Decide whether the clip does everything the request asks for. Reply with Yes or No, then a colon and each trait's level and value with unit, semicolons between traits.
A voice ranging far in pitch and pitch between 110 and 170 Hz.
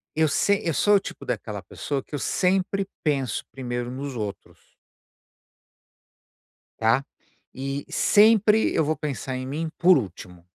Yes: wide, 6.6 semitones; medium, 140 Hz